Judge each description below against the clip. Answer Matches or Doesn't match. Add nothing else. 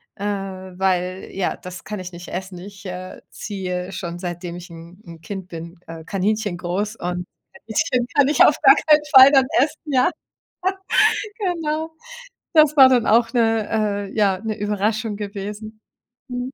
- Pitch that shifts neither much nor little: Matches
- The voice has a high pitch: Matches